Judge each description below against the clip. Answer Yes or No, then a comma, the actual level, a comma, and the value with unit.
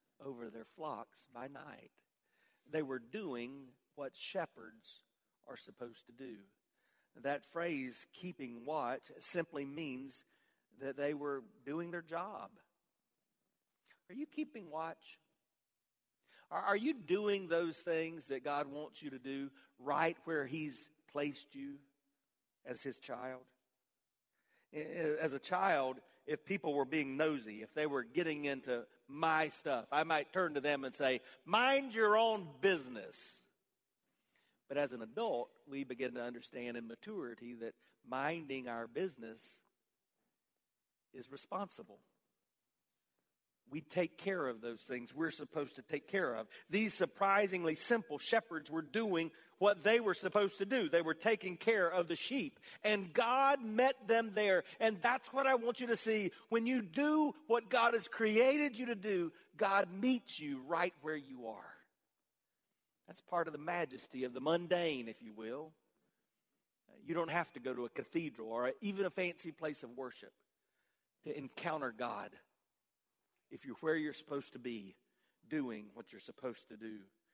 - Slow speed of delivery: No, average, 150 wpm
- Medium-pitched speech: Yes, medium, 155 Hz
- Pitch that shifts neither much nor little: No, wide, 6.8 semitones